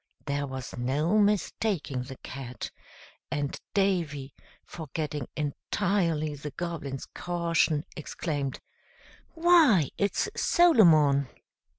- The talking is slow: Yes, slow, 85 wpm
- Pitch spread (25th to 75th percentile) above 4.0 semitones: Yes, average, 4.7 semitones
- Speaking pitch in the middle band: Yes, medium, 155 Hz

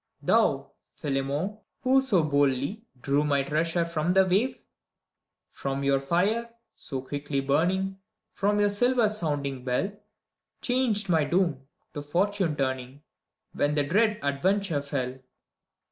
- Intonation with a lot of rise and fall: Yes, wide, 6.4 semitones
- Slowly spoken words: Yes, slow, 125 wpm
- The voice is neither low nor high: Yes, medium, 160 Hz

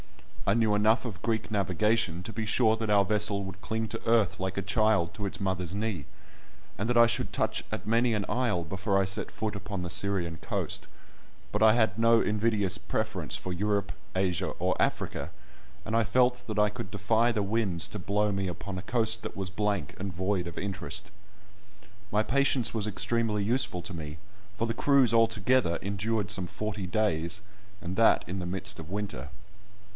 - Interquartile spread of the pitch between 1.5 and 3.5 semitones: Yes, average, 3.0 semitones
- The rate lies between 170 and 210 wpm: Yes, average, 190 wpm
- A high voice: No, low, 105 Hz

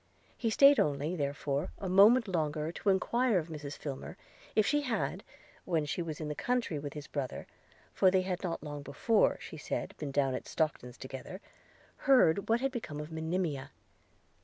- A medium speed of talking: Yes, average, 180 wpm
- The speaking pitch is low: No, medium, 160 Hz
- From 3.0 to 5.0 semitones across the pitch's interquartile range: No, wide, 5.4 semitones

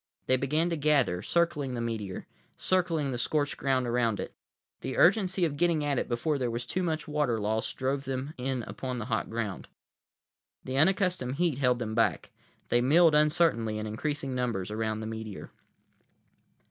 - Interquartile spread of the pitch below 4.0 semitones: No, average, 4.7 semitones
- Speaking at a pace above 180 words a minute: No, average, 170 wpm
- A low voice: Yes, low, 130 Hz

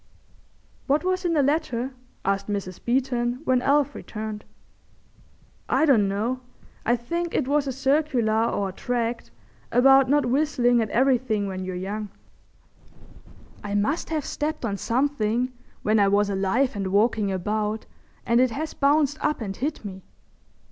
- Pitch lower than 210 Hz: No, high, 240 Hz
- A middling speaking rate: Yes, average, 150 wpm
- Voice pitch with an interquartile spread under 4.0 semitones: No, average, 5.1 semitones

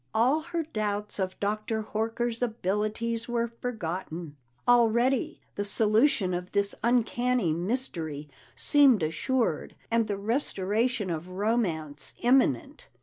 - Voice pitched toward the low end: No, high, 220 Hz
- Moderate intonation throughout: Yes, average, 4.4 semitones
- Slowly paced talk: Yes, slow, 110 wpm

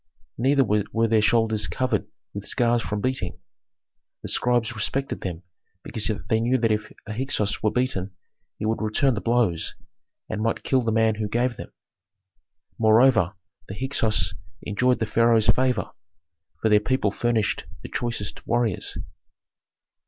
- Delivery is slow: No, average, 145 wpm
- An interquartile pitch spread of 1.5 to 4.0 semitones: Yes, narrow, 2.5 semitones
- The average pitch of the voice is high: No, low, 115 Hz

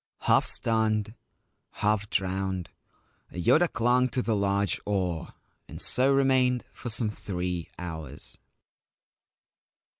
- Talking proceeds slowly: Yes, slow, 100 wpm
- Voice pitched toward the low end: Yes, low, 105 Hz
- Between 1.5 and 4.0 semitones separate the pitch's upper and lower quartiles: No, average, 4.7 semitones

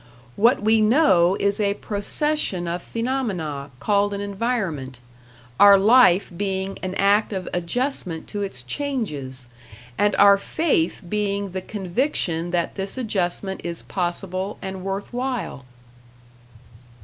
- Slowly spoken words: Yes, slow, 125 wpm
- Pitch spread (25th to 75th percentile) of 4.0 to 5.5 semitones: No, average, 3.5 semitones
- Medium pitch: No, high, 200 Hz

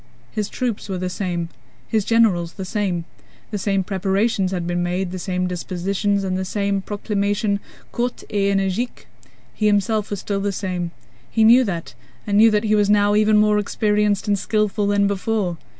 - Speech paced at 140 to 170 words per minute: No, average, 180 wpm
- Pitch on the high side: Yes, high, 200 Hz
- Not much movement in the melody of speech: Yes, narrow, 2.1 semitones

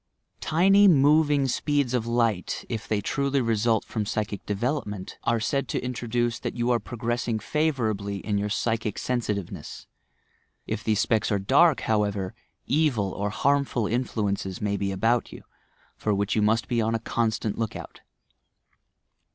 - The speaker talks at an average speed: Yes, average, 160 wpm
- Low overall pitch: Yes, low, 115 Hz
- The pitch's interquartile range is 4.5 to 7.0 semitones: No, average, 3.5 semitones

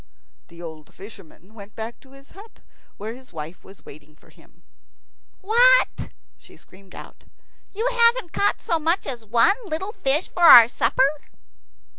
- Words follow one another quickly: No, average, 155 wpm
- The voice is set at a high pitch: Yes, very high, 260 Hz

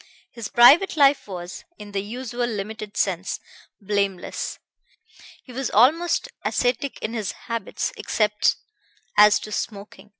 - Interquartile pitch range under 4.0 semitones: Yes, average, 3.6 semitones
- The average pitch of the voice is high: Yes, high, 215 Hz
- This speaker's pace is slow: Yes, slow, 125 wpm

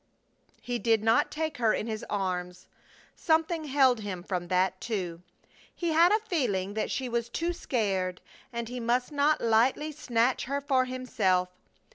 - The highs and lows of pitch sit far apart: Yes, wide, 6.2 semitones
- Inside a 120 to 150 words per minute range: No, average, 160 wpm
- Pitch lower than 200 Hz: No, high, 235 Hz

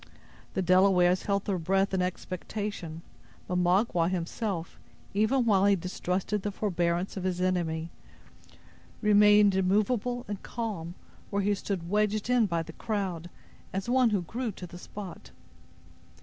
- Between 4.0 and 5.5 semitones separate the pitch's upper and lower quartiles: No, average, 2.8 semitones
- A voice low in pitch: No, high, 190 Hz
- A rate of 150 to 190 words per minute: No, average, 140 wpm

